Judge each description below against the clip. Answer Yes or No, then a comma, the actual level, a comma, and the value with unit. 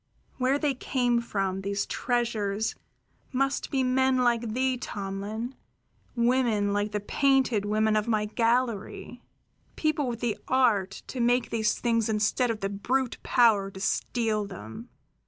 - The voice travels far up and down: No, average, 3.4 semitones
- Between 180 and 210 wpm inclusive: No, average, 140 wpm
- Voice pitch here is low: No, high, 230 Hz